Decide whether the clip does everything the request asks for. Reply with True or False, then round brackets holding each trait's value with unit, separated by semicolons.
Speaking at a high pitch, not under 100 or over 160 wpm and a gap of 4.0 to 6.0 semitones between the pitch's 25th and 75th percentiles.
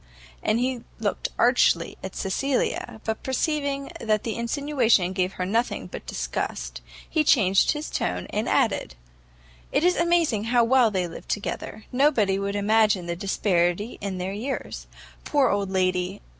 True (215 Hz; 150 wpm; 5.4 semitones)